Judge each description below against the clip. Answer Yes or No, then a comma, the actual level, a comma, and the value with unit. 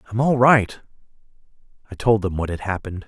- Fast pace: No, average, 175 wpm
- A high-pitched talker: No, low, 105 Hz